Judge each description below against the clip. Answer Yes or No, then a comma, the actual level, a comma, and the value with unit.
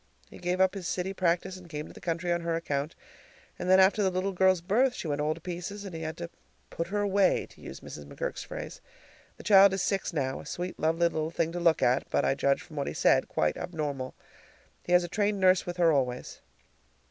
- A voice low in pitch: No, medium, 175 Hz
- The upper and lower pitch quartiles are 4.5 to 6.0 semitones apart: No, average, 3.0 semitones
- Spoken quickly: Yes, fast, 240 wpm